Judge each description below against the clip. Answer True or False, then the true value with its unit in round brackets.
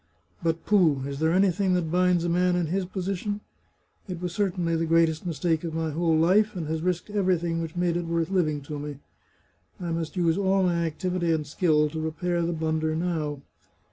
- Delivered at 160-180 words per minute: False (200 wpm)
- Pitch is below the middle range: False (170 Hz)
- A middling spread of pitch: False (2.2 semitones)